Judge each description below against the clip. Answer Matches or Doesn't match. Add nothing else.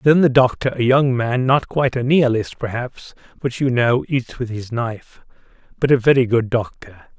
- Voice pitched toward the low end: Matches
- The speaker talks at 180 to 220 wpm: Matches